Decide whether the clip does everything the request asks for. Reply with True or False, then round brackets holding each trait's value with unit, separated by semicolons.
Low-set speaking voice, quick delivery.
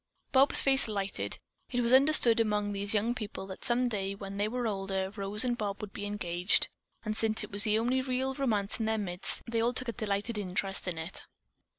False (210 Hz; 215 wpm)